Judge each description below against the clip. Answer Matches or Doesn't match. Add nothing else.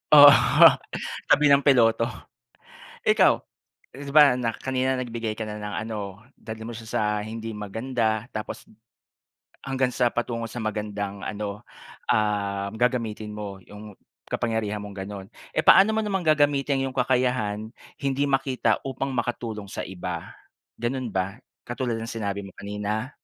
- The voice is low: Matches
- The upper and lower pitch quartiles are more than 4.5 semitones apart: Doesn't match